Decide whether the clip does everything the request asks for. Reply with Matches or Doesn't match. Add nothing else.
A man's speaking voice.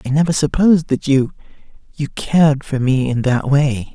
Matches